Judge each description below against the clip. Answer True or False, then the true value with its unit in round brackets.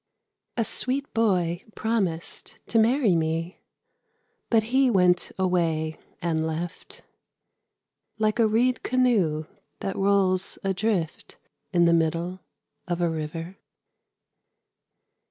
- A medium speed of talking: False (100 wpm)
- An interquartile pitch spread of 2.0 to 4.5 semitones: False (4.9 semitones)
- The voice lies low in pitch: False (185 Hz)